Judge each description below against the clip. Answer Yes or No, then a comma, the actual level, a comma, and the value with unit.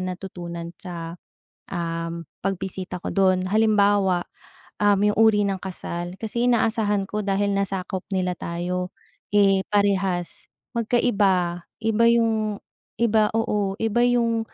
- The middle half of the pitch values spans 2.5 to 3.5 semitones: Yes, average, 3.1 semitones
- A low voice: No, high, 195 Hz